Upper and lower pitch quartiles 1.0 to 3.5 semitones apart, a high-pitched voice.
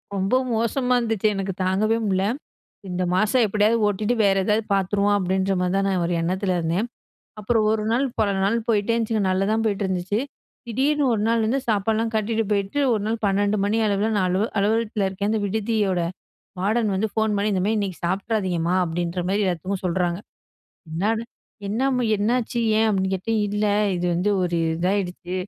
Yes: average, 2.8 semitones; high, 205 Hz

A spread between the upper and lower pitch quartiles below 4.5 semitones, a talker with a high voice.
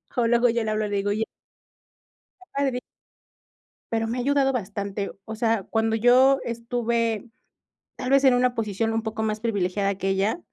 Yes: narrow, 2.6 semitones; high, 225 Hz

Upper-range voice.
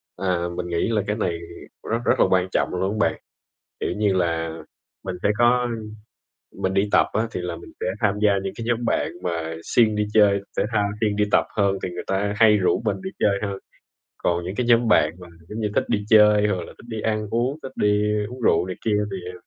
No: low, 105 Hz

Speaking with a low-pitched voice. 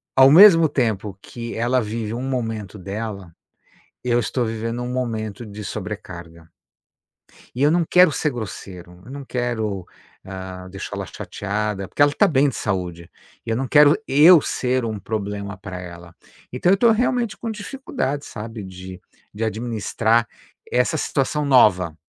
Yes: low, 115 Hz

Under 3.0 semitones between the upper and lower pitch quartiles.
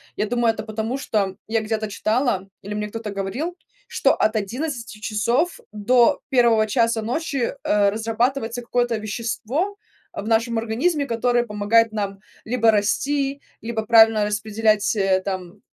Yes: narrow, 2.5 semitones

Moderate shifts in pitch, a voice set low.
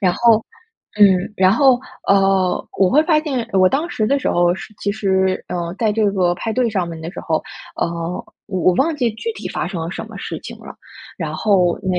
No: average, 4.2 semitones; high, 195 Hz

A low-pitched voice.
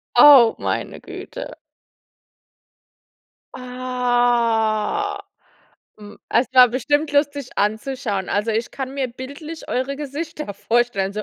No: very high, 250 Hz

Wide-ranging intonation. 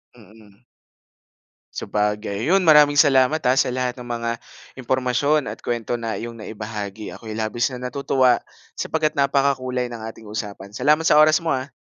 No: average, 3.9 semitones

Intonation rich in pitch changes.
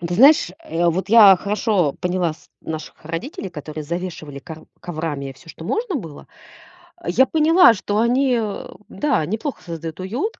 Yes: wide, 6.6 semitones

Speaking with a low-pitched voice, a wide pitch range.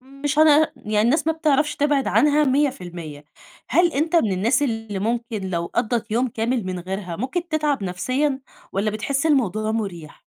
No: high, 240 Hz; wide, 6.4 semitones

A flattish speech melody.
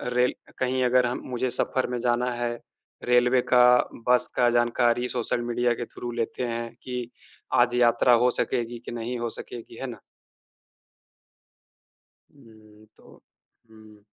Yes: narrow, 1.0 semitones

